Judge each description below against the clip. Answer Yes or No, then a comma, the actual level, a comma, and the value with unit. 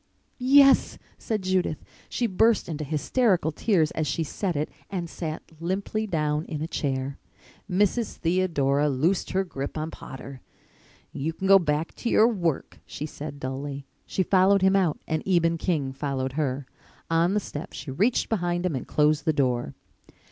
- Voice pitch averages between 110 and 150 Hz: No, medium, 160 Hz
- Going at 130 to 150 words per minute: No, average, 165 wpm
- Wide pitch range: No, average, 4.7 semitones